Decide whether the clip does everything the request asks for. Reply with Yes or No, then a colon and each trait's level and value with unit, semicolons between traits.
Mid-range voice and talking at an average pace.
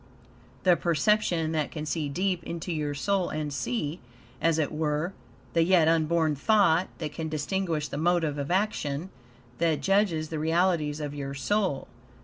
Yes: medium, 160 Hz; average, 155 wpm